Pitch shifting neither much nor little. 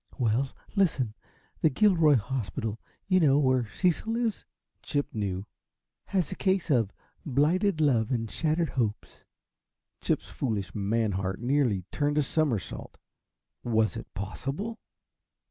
No: wide, 6.3 semitones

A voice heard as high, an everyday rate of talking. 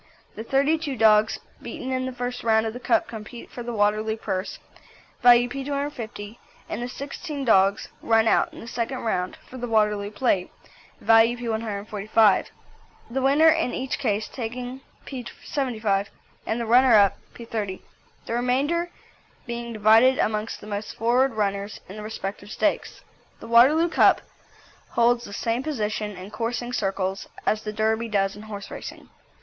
Yes: high, 230 Hz; average, 155 wpm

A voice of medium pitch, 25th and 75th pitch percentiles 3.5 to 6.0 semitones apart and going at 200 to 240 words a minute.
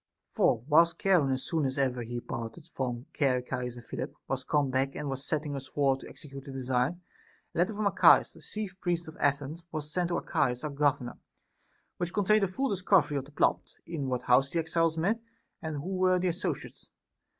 Yes: medium, 145 Hz; average, 4.6 semitones; fast, 205 wpm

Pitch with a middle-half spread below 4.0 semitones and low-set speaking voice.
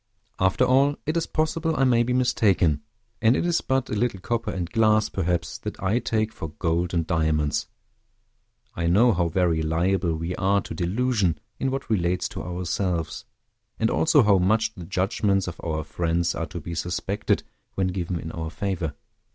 No: average, 5.0 semitones; very low, 95 Hz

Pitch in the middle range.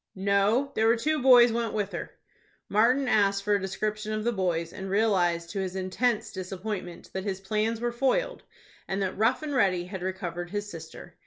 No: high, 205 Hz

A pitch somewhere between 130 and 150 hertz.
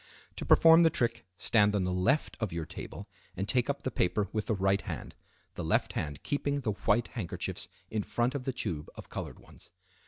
No: low, 110 Hz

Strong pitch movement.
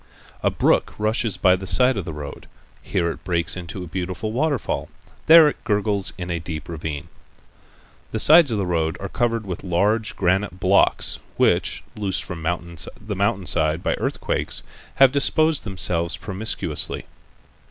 No: average, 4.2 semitones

